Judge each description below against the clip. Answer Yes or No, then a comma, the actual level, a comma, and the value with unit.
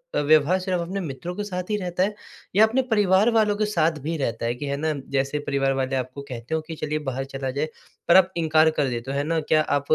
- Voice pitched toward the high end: No, medium, 155 Hz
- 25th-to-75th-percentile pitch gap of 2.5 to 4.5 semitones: No, average, 5.2 semitones